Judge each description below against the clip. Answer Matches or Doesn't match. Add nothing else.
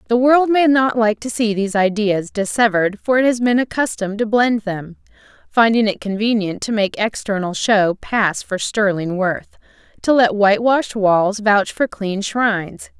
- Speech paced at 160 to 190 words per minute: Matches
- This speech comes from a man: Doesn't match